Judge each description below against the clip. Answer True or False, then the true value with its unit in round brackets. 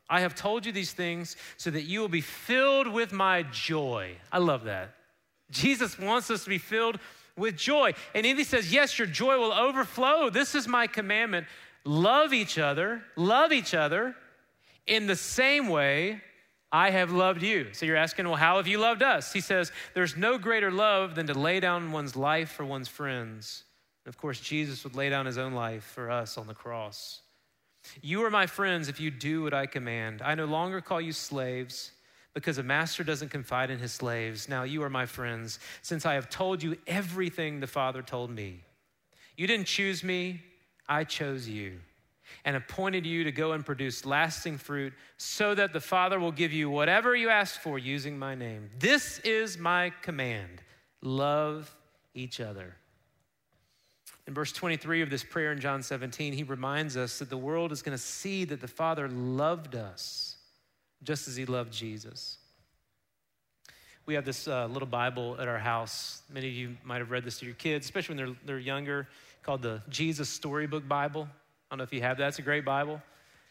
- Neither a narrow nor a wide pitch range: False (5.9 semitones)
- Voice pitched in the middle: True (150 Hz)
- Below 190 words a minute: False (195 wpm)